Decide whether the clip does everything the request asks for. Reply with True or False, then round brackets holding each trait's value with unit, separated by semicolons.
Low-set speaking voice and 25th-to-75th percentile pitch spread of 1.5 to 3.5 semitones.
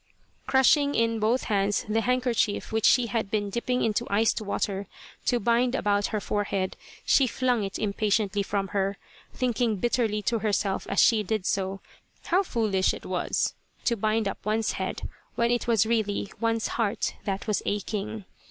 False (215 Hz; 2.6 semitones)